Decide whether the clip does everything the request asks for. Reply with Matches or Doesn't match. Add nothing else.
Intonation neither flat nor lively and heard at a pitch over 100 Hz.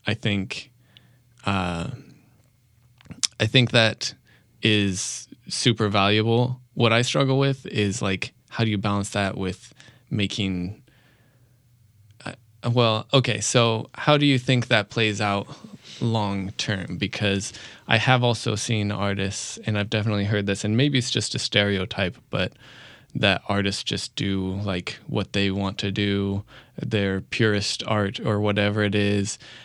Matches